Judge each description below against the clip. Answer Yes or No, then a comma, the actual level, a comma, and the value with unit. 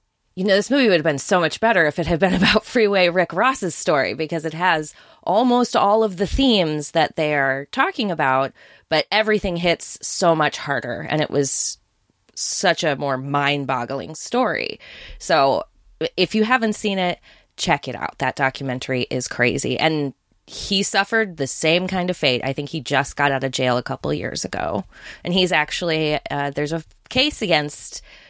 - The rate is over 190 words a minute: No, average, 185 wpm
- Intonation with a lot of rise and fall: Yes, wide, 5.7 semitones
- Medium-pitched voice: Yes, medium, 160 Hz